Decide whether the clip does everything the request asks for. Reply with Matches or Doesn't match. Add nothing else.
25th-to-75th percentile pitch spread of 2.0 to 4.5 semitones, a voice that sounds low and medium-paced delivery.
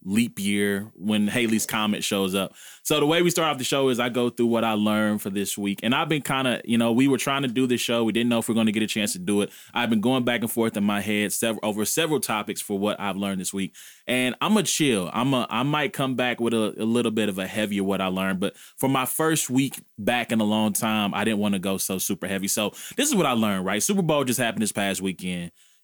Doesn't match